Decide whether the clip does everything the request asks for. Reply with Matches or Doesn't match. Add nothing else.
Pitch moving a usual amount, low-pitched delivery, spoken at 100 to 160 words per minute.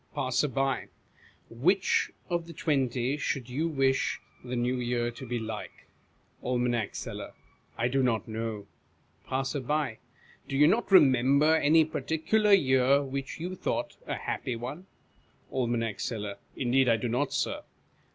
Matches